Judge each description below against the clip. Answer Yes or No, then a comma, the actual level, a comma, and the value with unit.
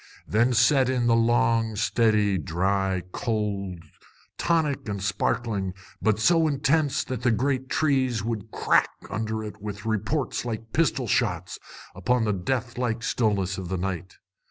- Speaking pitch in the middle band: No, low, 110 Hz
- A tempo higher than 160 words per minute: No, average, 145 wpm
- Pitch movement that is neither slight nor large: Yes, average, 4.1 semitones